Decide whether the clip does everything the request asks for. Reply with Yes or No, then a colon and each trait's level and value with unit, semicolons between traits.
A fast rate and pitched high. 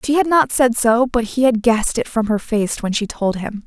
Yes: fast, 280 wpm; high, 235 Hz